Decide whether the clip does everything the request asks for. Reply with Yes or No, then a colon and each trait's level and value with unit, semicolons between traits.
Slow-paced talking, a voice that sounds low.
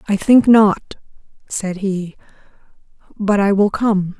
No: slow, 130 wpm; high, 200 Hz